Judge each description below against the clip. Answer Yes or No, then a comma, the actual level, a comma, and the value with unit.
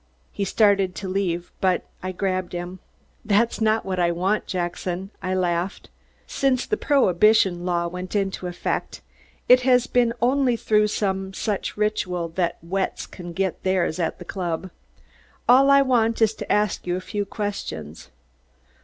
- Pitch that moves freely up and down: No, average, 3.4 semitones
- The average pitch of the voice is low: No, high, 190 Hz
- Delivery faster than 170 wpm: No, average, 155 wpm